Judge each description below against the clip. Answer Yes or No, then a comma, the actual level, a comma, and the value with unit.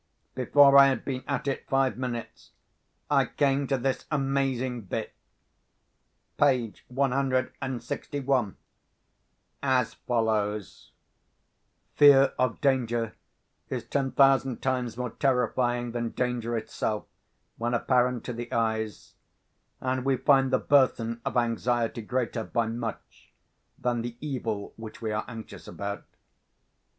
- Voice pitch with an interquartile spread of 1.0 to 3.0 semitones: Yes, narrow, 2.6 semitones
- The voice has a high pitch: No, low, 125 Hz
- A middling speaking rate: No, slow, 120 wpm